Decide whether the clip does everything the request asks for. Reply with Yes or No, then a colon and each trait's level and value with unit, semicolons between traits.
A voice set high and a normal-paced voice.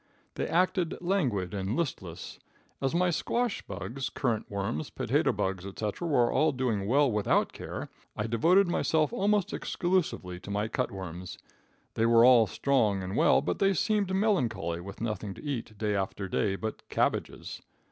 No: low, 115 Hz; average, 160 wpm